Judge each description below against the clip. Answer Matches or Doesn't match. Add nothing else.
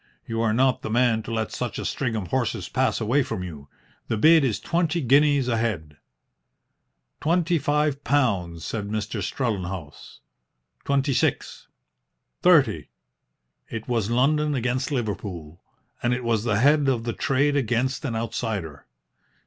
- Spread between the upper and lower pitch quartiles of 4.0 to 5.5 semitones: Matches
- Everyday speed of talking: Matches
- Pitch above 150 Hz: Doesn't match